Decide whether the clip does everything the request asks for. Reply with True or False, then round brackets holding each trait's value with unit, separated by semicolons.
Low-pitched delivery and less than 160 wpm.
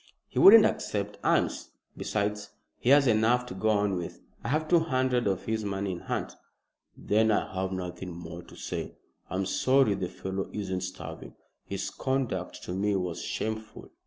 False (105 Hz; 170 wpm)